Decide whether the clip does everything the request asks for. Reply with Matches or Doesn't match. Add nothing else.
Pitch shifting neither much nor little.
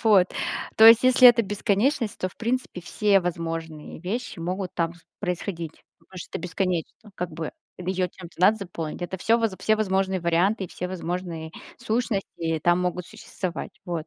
Matches